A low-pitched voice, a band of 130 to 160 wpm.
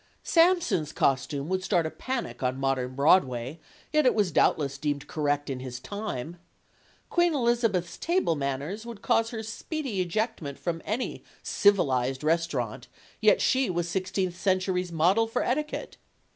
No: medium, 180 Hz; average, 145 wpm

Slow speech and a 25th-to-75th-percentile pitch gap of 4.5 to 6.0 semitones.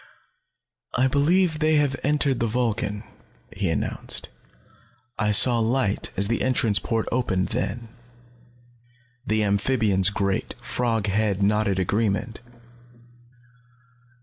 No: slow, 105 wpm; average, 4.1 semitones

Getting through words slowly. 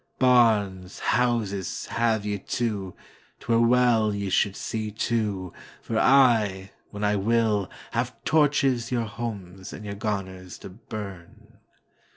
Yes: slow, 115 wpm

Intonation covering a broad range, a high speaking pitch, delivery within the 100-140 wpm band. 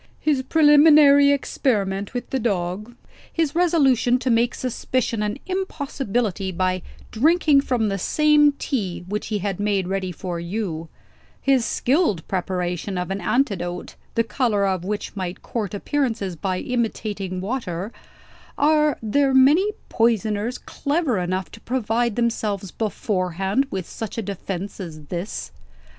Yes: wide, 5.9 semitones; high, 220 Hz; slow, 135 wpm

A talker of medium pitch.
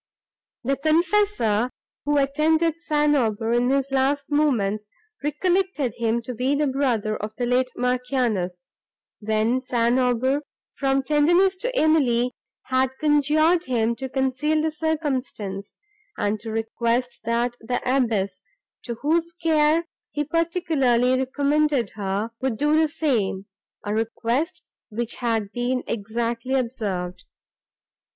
No: very high, 255 Hz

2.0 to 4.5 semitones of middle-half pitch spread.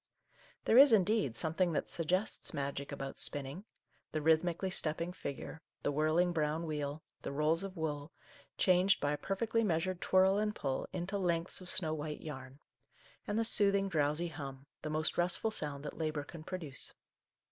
Yes: average, 4.0 semitones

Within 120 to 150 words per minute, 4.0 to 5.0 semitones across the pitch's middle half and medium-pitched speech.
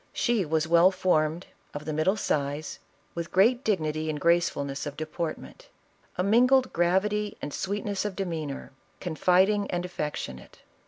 Yes: average, 140 wpm; average, 4.3 semitones; medium, 175 Hz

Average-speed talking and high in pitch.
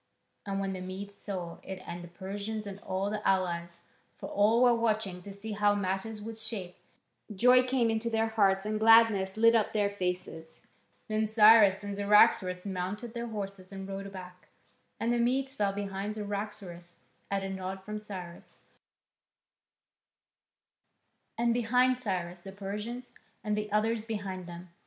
Yes: average, 160 wpm; high, 205 Hz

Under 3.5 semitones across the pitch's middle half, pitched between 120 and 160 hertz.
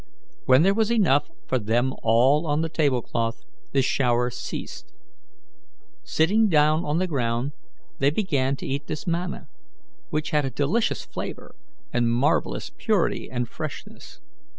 No: average, 4.8 semitones; medium, 140 Hz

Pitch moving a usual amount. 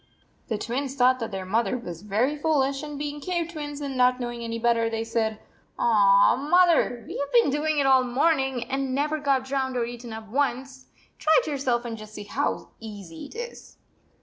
Yes: average, 3.9 semitones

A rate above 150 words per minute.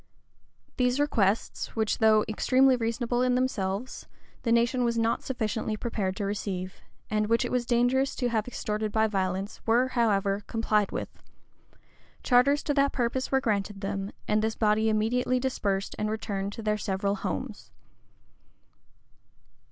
No: average, 145 wpm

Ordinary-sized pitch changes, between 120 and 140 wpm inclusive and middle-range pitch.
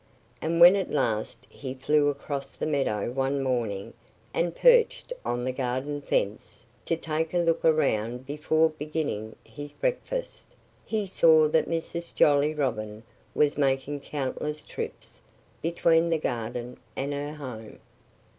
Yes: average, 4.0 semitones; slow, 135 wpm; medium, 145 Hz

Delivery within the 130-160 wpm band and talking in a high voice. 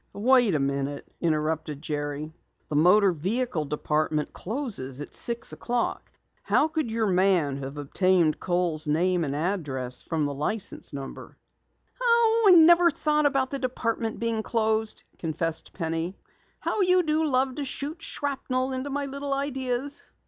Yes: average, 140 wpm; high, 205 Hz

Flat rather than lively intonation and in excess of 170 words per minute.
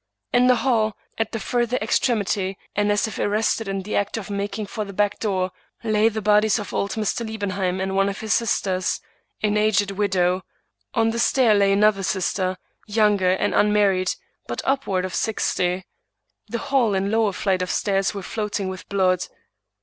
Yes: narrow, 2.3 semitones; average, 180 wpm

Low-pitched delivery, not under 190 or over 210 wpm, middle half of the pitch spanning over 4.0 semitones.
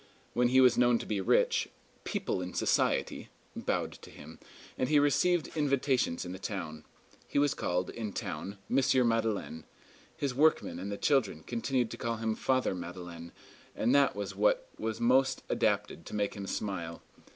No: low, 115 Hz; average, 170 wpm; wide, 5.6 semitones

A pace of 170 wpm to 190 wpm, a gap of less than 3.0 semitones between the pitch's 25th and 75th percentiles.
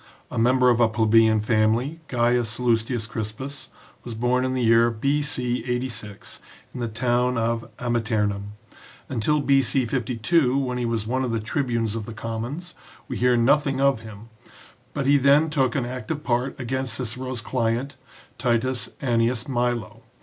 No: average, 155 wpm; narrow, 2.4 semitones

